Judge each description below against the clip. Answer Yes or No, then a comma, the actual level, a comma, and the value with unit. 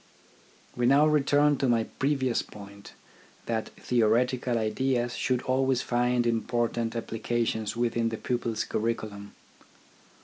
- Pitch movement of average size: No, narrow, 2.1 semitones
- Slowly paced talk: Yes, slow, 110 wpm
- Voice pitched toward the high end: No, low, 120 Hz